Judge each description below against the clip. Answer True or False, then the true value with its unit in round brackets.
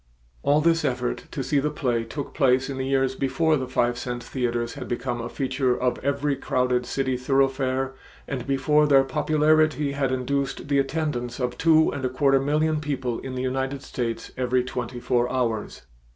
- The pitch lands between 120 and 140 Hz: True (135 Hz)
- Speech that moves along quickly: False (180 wpm)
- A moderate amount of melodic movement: False (2.2 semitones)